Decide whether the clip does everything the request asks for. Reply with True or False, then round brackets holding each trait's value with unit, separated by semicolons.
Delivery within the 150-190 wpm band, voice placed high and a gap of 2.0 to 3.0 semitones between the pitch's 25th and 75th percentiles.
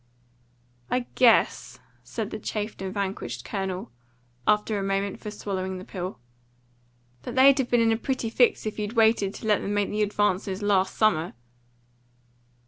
True (160 wpm; 205 Hz; 2.5 semitones)